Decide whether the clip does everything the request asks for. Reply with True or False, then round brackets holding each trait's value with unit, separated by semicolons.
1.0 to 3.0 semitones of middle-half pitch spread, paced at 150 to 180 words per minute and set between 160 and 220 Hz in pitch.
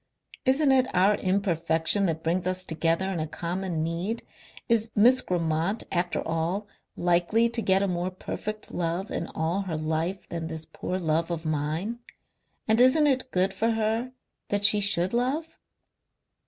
False (4.8 semitones; 160 wpm; 185 Hz)